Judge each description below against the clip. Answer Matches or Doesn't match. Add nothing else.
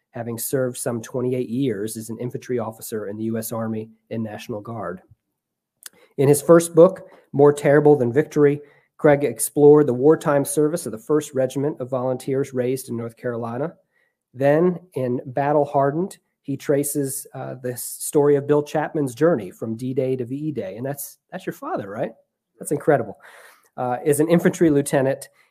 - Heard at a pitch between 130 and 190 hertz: Matches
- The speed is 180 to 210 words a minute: Doesn't match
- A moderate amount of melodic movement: Matches